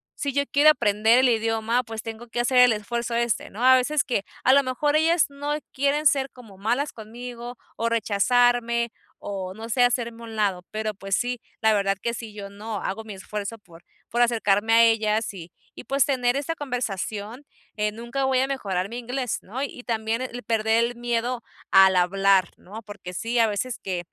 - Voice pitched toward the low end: No, high, 230 Hz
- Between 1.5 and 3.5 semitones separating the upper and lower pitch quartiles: Yes, average, 2.9 semitones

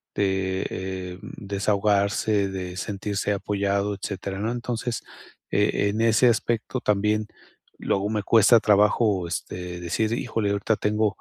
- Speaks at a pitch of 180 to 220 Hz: No, low, 100 Hz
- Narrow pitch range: Yes, narrow, 1.9 semitones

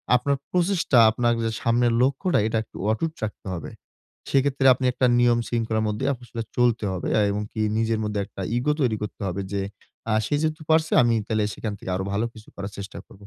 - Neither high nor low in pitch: No, low, 115 Hz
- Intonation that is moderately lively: Yes, average, 3.9 semitones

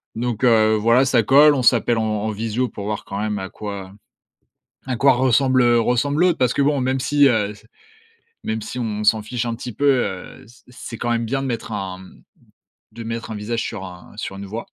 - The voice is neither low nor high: No, low, 115 Hz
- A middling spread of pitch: Yes, average, 3.3 semitones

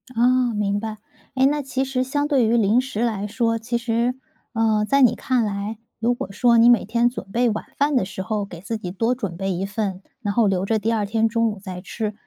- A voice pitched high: Yes, high, 225 Hz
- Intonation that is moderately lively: Yes, average, 3.0 semitones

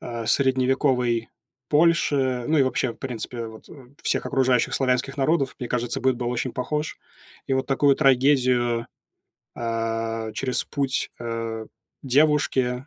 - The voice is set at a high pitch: No, low, 130 Hz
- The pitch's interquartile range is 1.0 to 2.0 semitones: No, narrow, 2.5 semitones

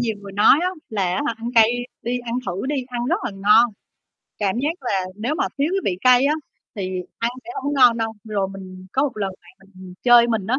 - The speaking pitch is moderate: No, high, 225 Hz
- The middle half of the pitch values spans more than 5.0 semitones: No, average, 4.3 semitones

